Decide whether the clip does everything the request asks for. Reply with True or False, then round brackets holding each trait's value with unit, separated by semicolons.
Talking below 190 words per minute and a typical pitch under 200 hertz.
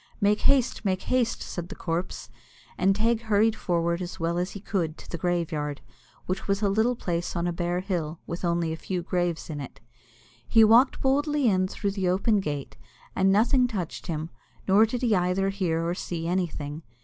False (195 wpm; 185 Hz)